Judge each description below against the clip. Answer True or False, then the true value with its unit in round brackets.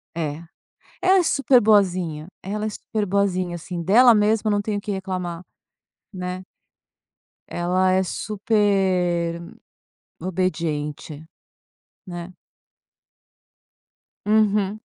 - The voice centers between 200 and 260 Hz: False (190 Hz)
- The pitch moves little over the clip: False (3.2 semitones)